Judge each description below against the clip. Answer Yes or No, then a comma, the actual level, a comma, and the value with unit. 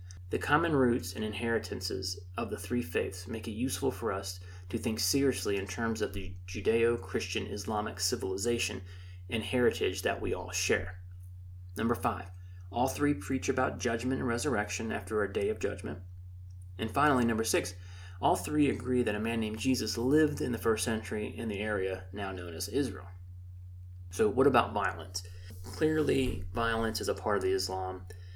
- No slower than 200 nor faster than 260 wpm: No, average, 170 wpm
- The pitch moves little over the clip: No, average, 4.4 semitones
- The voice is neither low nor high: No, low, 100 Hz